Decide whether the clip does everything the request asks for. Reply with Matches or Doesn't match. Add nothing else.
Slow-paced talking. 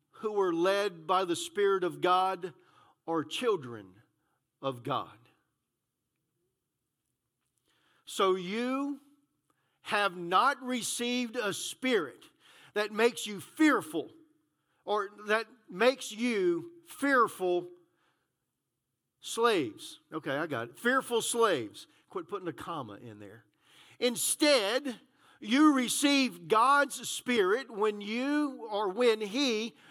Matches